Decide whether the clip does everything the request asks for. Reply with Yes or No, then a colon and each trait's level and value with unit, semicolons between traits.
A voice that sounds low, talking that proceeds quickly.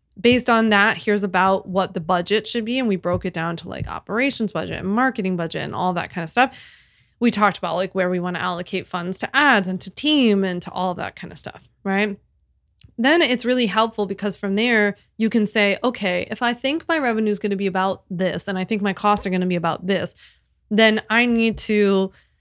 No: high, 200 Hz; fast, 240 wpm